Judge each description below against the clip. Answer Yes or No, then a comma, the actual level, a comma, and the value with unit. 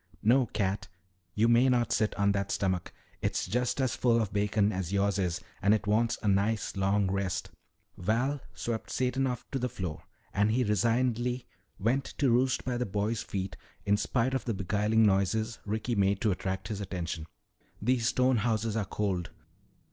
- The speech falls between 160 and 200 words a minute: Yes, average, 180 wpm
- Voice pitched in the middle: No, low, 105 Hz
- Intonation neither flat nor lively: Yes, average, 3.4 semitones